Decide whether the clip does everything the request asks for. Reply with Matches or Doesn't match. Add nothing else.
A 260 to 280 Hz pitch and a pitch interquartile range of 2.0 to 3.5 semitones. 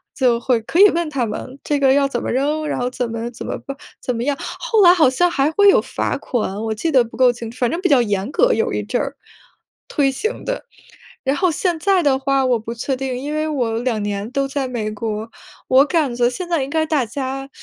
Doesn't match